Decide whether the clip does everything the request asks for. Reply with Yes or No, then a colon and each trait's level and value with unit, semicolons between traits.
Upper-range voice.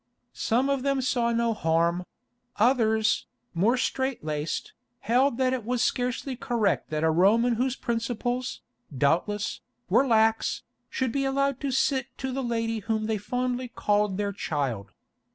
Yes: high, 235 Hz